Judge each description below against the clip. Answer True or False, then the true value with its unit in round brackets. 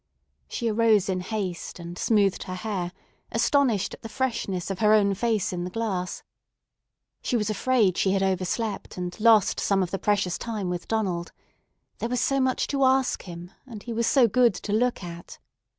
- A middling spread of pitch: True (4.0 semitones)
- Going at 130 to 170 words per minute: False (185 wpm)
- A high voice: True (205 Hz)